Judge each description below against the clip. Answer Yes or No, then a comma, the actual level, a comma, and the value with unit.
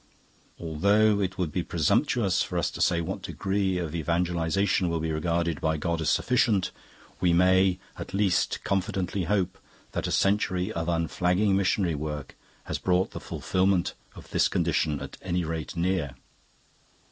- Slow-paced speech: No, average, 155 wpm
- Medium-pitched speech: No, very low, 90 Hz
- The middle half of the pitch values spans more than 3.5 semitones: No, average, 2.8 semitones